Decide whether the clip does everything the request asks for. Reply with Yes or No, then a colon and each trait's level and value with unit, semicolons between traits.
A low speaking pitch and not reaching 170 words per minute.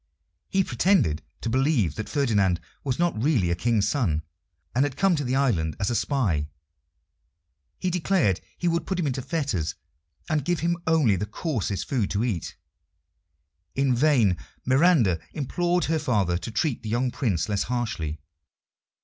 Yes: low, 125 Hz; average, 160 wpm